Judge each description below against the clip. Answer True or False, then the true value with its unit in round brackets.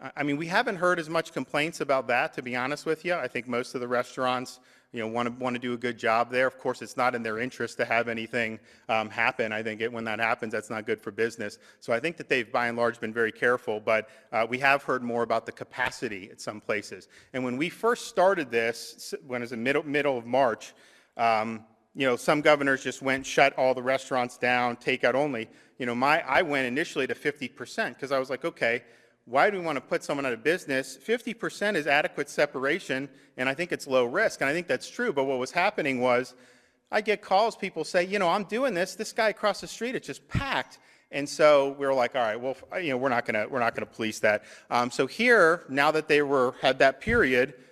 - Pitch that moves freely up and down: False (4.0 semitones)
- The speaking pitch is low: True (130 Hz)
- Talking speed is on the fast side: True (245 wpm)